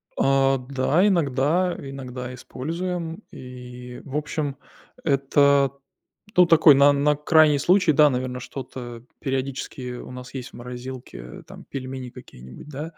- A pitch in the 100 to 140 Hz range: Yes, low, 135 Hz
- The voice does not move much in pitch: No, average, 3.0 semitones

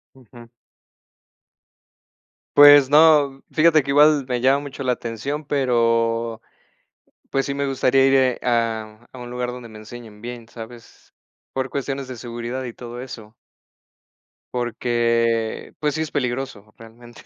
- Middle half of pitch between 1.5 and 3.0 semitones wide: Yes, average, 2.7 semitones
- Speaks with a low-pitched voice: Yes, low, 125 Hz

